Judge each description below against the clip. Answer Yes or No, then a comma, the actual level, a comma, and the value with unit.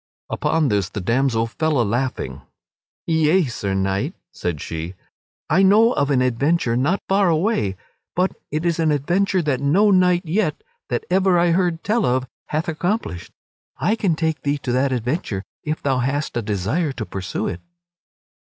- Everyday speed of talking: Yes, average, 170 wpm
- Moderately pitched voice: Yes, medium, 150 Hz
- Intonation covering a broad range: Yes, wide, 6.8 semitones